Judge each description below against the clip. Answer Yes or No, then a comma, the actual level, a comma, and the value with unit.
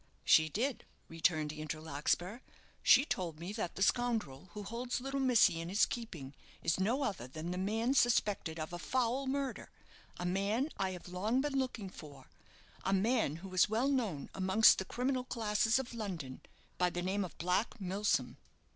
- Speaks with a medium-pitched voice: No, high, 200 Hz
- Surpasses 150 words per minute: Yes, average, 175 wpm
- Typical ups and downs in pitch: No, wide, 5.8 semitones